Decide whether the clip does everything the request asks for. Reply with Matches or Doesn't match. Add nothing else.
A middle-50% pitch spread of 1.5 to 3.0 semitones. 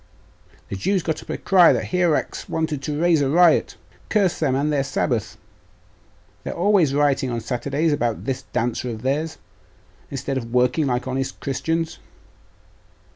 Doesn't match